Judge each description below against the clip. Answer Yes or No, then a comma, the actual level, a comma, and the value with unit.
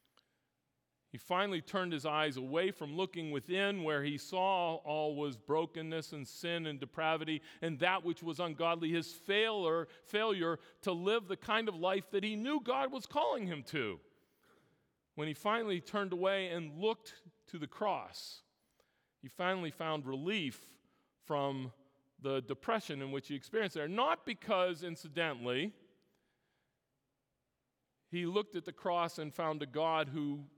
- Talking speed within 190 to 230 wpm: No, average, 150 wpm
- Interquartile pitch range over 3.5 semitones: Yes, average, 3.9 semitones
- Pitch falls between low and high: Yes, medium, 165 Hz